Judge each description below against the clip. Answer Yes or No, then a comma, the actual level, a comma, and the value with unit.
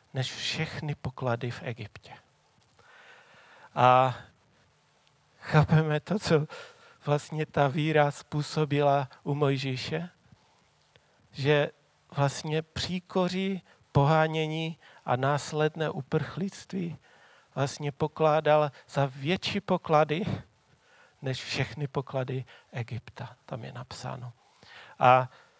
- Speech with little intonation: No, average, 3.1 semitones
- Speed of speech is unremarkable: No, slow, 80 wpm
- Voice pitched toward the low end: No, medium, 145 Hz